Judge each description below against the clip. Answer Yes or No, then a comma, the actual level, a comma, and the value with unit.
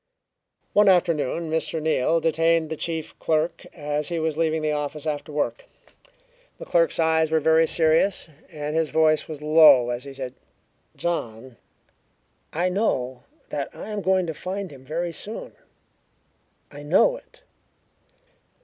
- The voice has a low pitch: No, medium, 160 Hz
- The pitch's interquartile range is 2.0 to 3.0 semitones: Yes, narrow, 2.4 semitones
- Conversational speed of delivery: Yes, average, 150 wpm